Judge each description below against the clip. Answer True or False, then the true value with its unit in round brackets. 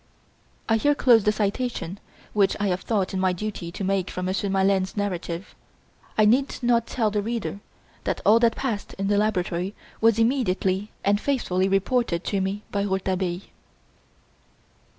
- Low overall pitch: False (200 Hz)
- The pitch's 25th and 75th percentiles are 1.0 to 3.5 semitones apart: True (2.9 semitones)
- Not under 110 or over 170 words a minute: True (160 wpm)